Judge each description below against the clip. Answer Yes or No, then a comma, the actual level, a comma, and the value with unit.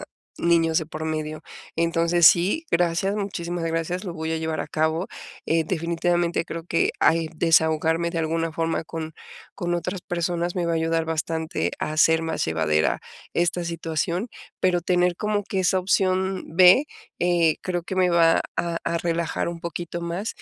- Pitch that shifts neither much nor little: No, narrow, 1.5 semitones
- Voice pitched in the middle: Yes, medium, 170 Hz